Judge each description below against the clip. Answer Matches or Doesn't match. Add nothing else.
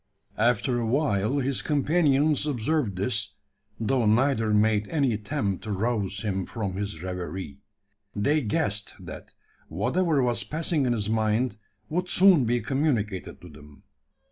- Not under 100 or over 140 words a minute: Matches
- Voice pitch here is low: Matches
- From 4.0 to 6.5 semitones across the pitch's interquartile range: Matches